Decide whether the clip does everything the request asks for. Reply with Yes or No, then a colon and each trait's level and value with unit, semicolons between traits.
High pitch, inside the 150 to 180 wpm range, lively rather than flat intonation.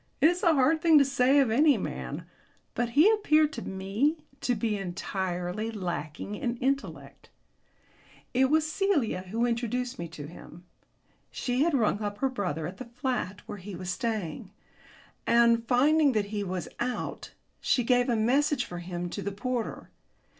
Yes: high, 235 Hz; average, 170 wpm; wide, 5.8 semitones